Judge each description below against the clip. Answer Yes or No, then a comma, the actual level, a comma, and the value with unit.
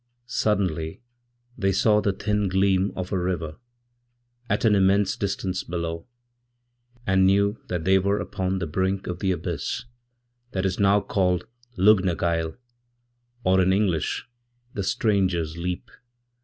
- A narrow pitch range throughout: Yes, narrow, 2.2 semitones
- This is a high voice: No, very low, 95 Hz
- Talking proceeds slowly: Yes, slow, 130 wpm